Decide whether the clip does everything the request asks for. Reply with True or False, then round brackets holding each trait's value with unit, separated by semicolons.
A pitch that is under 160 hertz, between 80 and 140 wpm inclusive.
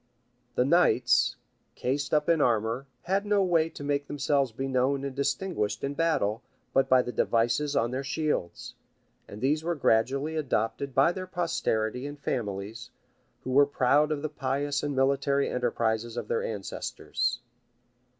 False (135 Hz; 155 wpm)